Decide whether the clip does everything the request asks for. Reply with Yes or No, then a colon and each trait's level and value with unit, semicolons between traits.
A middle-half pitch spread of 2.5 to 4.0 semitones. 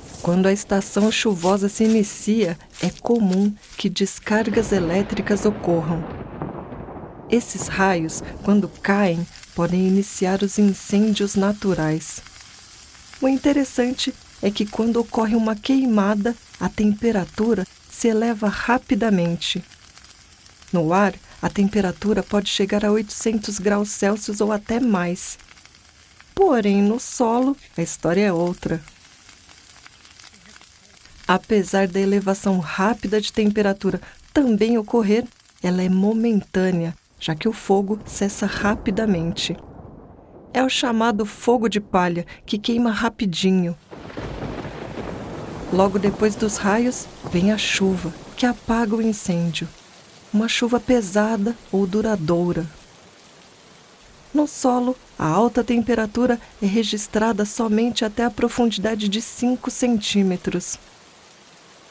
Yes: average, 3.4 semitones